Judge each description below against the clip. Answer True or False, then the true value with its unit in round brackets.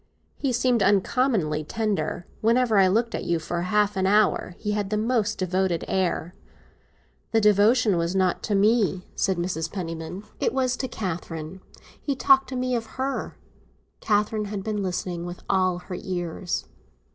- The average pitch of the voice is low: False (200 Hz)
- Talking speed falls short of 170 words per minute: True (160 wpm)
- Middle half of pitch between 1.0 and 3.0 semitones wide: False (3.8 semitones)